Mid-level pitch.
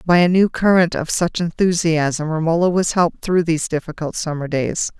Yes: medium, 165 Hz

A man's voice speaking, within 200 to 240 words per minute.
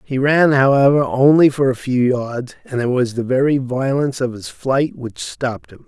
Yes: male; fast, 205 wpm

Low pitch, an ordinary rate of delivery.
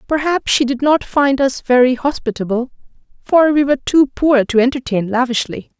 No: very high, 260 Hz; average, 165 wpm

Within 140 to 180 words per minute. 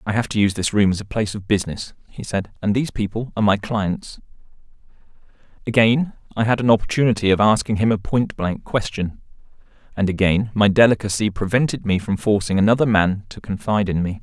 No: average, 190 wpm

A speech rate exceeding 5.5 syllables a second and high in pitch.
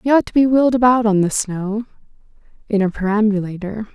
Yes: 6.0 syllables/s; high, 215 Hz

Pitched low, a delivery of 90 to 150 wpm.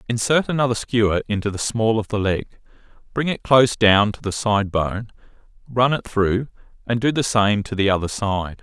No: low, 110 Hz; average, 195 wpm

